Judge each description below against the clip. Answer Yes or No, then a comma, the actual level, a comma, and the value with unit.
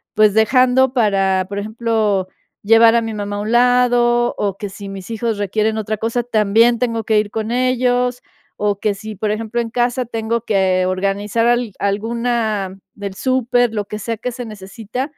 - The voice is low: No, high, 220 Hz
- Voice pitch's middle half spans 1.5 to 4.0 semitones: Yes, average, 2.8 semitones